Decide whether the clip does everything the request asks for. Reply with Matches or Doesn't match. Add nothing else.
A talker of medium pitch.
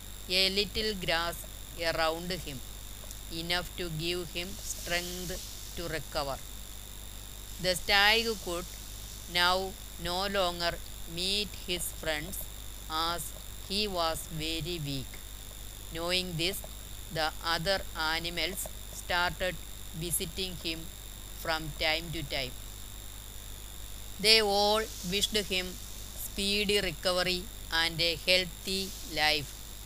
Matches